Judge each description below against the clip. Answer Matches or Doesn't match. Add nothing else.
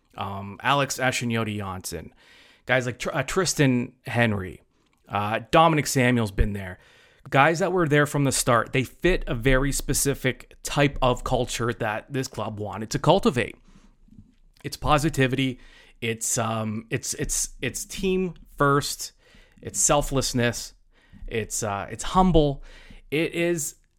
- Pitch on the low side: Matches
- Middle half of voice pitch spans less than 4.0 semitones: Doesn't match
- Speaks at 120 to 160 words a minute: Matches